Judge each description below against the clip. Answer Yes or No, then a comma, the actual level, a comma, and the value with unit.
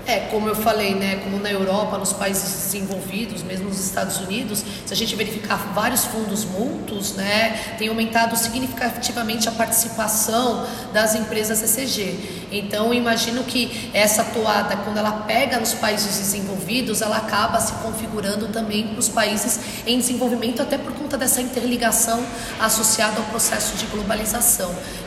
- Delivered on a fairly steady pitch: Yes, narrow, 2.0 semitones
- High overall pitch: Yes, high, 220 Hz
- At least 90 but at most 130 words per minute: No, average, 145 wpm